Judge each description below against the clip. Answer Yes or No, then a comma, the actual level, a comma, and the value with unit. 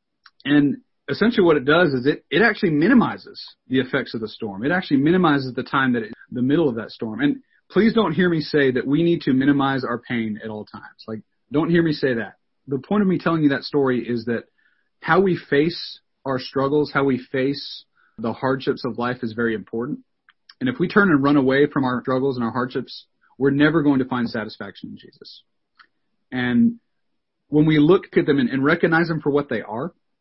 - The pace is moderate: No, fast, 215 wpm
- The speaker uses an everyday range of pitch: Yes, average, 4.6 semitones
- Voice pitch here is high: No, medium, 140 Hz